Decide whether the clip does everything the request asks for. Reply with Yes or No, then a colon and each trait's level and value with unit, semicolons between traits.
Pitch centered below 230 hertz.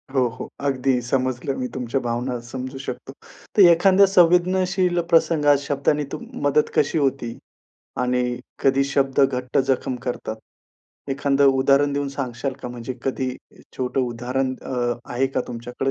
Yes: low, 135 Hz